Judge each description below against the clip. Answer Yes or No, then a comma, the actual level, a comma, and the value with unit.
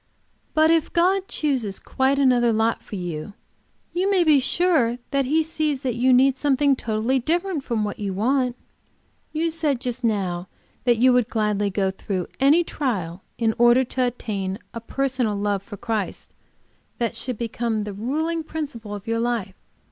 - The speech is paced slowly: No, average, 165 wpm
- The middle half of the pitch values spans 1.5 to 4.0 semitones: No, average, 4.9 semitones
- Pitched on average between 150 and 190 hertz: No, high, 245 Hz